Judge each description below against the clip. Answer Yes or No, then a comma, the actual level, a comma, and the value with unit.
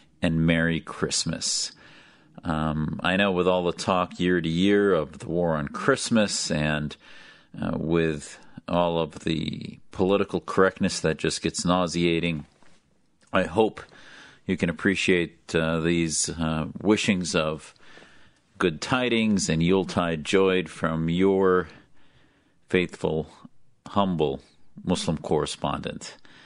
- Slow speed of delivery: Yes, slow, 115 wpm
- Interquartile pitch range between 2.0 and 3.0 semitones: Yes, narrow, 2.6 semitones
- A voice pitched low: Yes, very low, 85 Hz